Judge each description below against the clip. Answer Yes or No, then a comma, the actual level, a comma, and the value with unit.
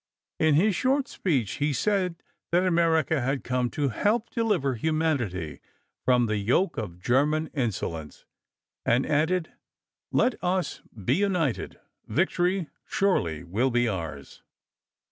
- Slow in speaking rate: Yes, slow, 125 wpm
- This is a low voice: No, medium, 150 Hz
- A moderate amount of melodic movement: No, wide, 7.3 semitones